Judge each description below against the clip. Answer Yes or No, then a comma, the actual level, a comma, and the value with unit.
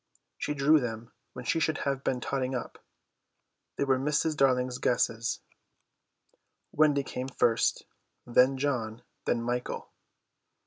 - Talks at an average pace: No, slow, 125 wpm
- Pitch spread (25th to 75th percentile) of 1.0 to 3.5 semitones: Yes, narrow, 2.5 semitones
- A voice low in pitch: Yes, low, 130 Hz